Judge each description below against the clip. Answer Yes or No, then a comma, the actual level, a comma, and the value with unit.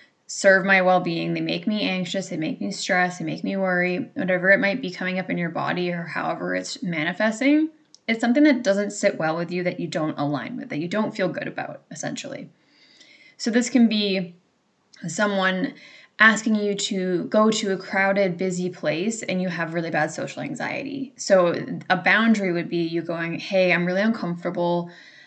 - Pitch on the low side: No, high, 190 Hz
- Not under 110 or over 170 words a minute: No, average, 190 wpm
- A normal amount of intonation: Yes, average, 3.7 semitones